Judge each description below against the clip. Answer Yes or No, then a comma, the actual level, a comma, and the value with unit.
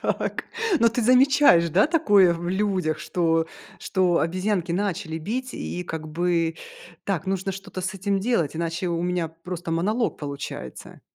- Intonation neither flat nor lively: Yes, average, 3.3 semitones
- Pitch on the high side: No, medium, 180 Hz